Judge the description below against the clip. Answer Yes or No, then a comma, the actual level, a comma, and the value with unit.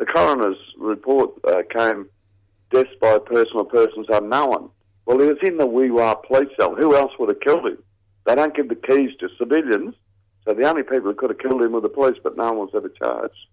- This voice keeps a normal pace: No, fast, 215 wpm